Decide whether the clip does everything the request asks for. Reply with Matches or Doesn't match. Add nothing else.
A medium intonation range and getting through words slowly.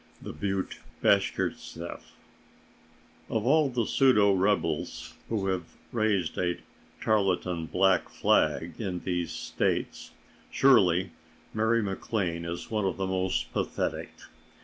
Matches